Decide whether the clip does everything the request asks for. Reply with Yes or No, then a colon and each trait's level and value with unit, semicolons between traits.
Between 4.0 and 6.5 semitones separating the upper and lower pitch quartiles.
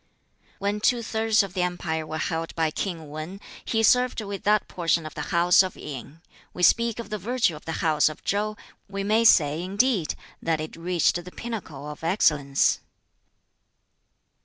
Yes: average, 5.0 semitones